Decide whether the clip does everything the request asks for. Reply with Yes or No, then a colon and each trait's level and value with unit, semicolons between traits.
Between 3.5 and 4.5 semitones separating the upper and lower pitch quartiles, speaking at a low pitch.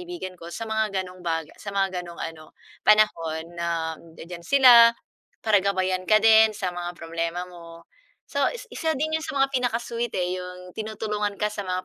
No: average, 4.2 semitones; high, 190 Hz